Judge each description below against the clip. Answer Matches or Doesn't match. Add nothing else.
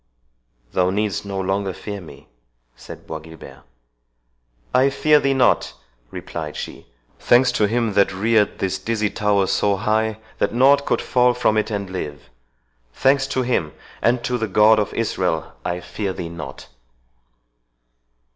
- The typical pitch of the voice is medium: Doesn't match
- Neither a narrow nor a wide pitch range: Matches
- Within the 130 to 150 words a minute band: Matches